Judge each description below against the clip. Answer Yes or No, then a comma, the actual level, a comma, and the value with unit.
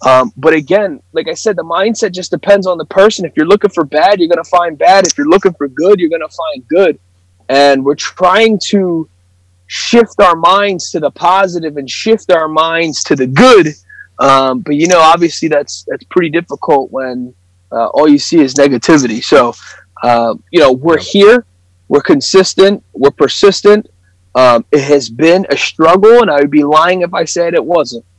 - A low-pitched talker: No, medium, 160 Hz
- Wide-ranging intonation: Yes, wide, 6.2 semitones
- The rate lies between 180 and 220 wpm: Yes, average, 190 wpm